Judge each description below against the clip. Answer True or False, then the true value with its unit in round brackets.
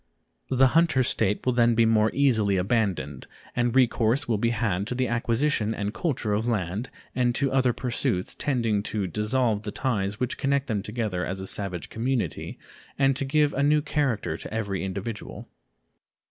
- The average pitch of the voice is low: True (115 Hz)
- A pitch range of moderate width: True (4.1 semitones)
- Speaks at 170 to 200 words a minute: True (175 wpm)